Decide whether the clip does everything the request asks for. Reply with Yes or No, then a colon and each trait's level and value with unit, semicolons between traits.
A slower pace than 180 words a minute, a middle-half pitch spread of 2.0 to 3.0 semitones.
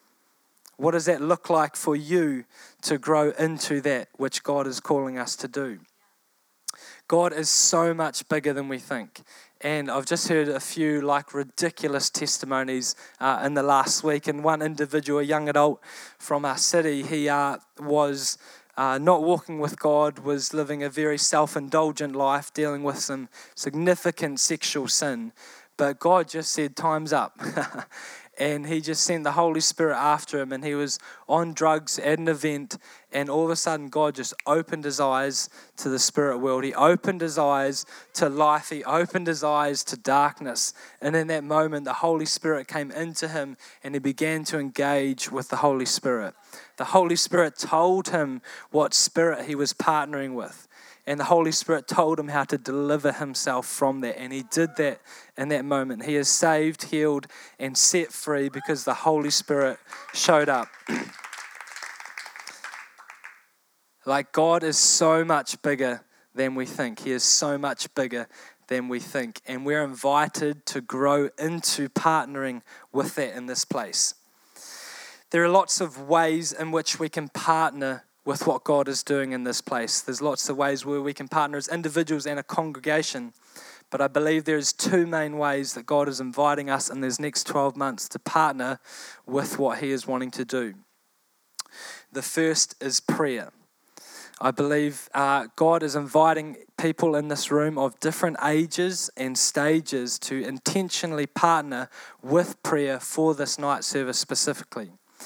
Yes: average, 170 wpm; narrow, 2.5 semitones